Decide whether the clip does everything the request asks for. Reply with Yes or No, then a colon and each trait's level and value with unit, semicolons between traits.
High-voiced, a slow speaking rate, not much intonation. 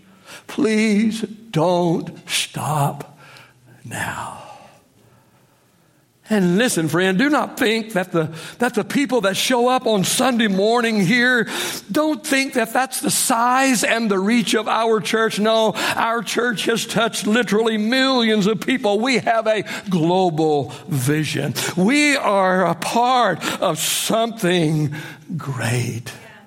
No: high, 215 Hz; slow, 125 wpm; average, 5.3 semitones